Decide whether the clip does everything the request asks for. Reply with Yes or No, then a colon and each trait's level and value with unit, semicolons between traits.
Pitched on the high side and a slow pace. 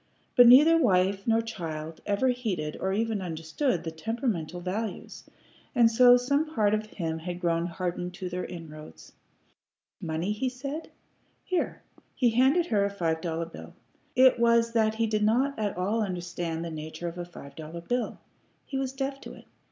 No: high, 200 Hz; average, 175 wpm